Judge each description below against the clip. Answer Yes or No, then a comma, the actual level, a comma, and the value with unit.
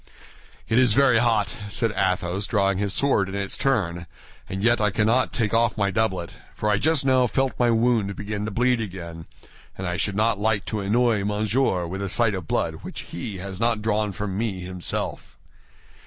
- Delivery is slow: No, average, 195 wpm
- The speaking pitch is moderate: No, low, 105 Hz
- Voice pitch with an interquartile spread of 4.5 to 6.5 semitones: No, average, 3.2 semitones